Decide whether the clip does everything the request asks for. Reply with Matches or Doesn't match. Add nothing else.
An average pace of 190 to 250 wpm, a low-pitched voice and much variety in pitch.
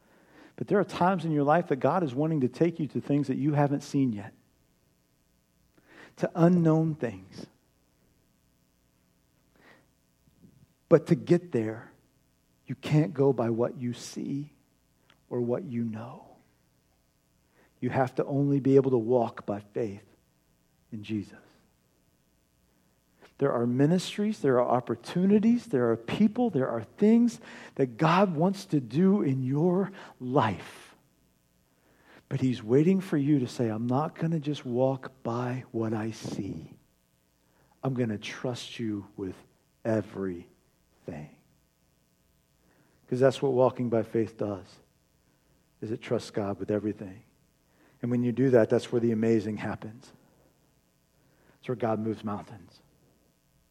Doesn't match